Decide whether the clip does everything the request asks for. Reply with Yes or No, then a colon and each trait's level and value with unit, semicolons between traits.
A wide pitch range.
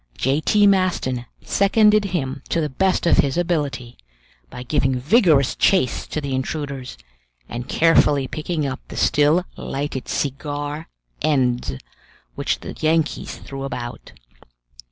No: average, 4.2 semitones